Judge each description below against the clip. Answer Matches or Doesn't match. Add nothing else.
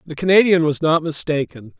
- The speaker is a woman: Doesn't match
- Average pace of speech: Matches